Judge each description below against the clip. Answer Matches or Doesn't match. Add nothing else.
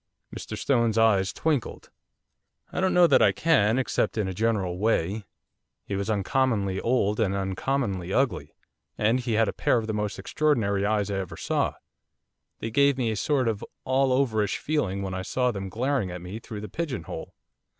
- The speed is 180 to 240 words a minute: Matches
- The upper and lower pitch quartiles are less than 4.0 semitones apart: Doesn't match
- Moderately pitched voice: Doesn't match